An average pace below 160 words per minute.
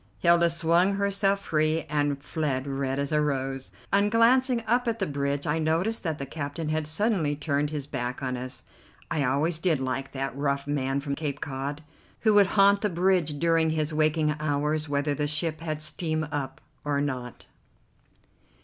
No: average, 175 wpm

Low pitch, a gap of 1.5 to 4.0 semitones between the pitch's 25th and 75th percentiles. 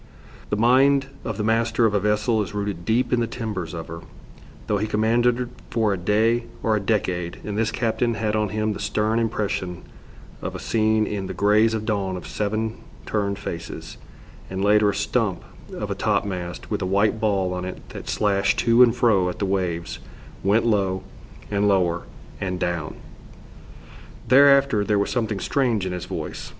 Yes: low, 105 Hz; average, 2.8 semitones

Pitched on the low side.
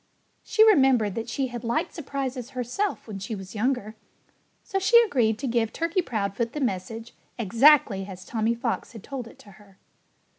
No: high, 235 Hz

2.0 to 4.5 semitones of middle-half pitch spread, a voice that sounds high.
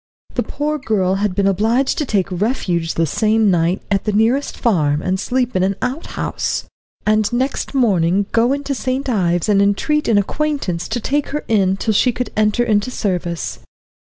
No: average, 5.1 semitones; high, 215 Hz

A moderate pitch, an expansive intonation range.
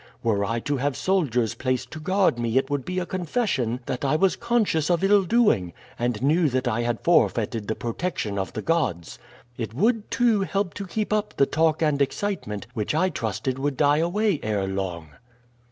Yes: medium, 145 Hz; wide, 8.2 semitones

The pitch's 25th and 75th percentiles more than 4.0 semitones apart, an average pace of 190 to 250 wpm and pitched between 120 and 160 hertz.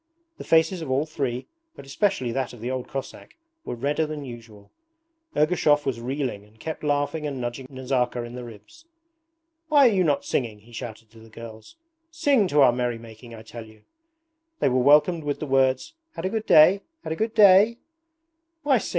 Yes: average, 5.2 semitones; average, 195 wpm; low, 135 Hz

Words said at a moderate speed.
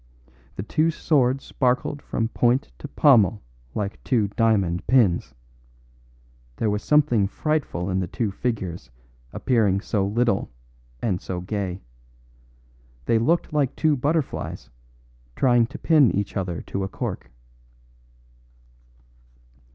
No: slow, 120 wpm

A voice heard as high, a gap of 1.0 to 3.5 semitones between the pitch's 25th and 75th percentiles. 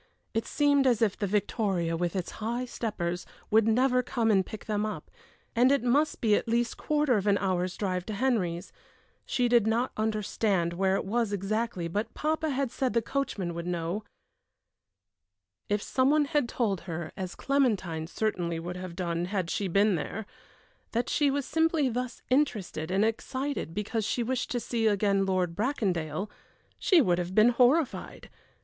No: high, 215 Hz; average, 5.2 semitones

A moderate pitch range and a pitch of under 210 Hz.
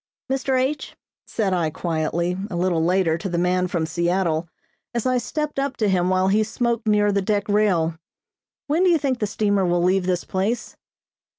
Yes: average, 4.6 semitones; high, 190 Hz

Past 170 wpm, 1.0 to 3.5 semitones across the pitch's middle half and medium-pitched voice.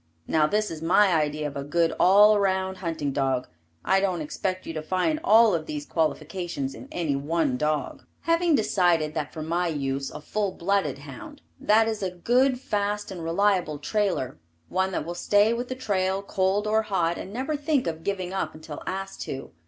No: average, 190 wpm; average, 5.0 semitones; medium, 180 Hz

